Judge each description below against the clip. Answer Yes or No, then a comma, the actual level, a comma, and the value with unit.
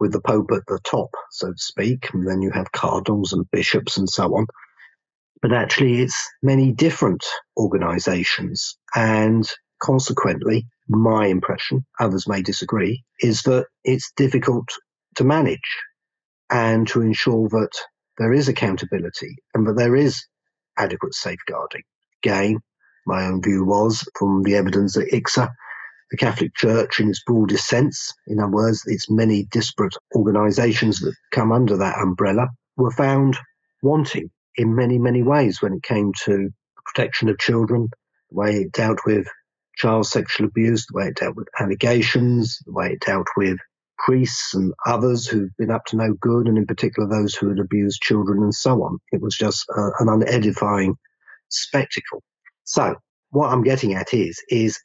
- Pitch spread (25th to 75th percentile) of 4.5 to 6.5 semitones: No, average, 3.3 semitones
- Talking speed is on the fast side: No, average, 160 wpm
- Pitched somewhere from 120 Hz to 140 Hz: No, low, 110 Hz